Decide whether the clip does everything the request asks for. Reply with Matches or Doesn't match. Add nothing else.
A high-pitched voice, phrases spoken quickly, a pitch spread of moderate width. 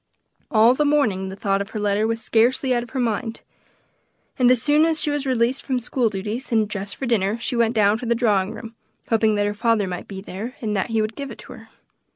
Matches